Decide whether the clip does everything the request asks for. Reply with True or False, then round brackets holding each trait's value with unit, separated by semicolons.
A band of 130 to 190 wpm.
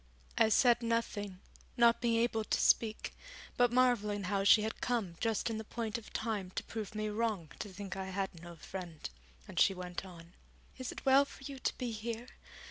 False (200 wpm)